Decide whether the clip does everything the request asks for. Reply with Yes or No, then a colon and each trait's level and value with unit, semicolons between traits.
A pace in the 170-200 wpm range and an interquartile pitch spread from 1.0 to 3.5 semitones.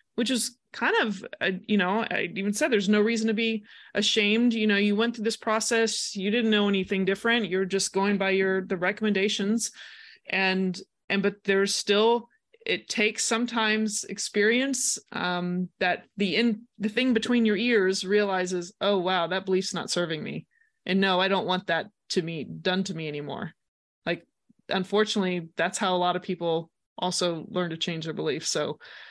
Yes: average, 180 wpm; average, 3.2 semitones